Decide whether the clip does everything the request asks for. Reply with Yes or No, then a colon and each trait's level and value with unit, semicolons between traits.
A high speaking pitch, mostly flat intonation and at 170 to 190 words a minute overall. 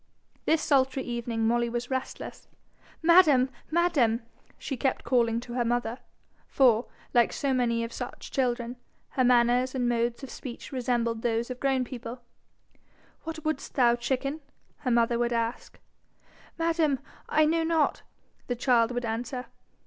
No: high, 245 Hz; narrow, 2.3 semitones; average, 145 wpm